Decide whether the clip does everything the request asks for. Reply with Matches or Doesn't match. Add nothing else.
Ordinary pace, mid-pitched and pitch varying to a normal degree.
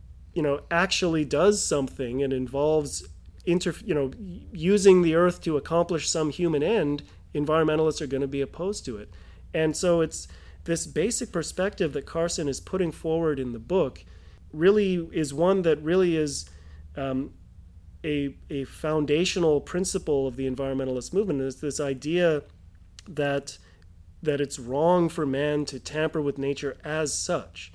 Matches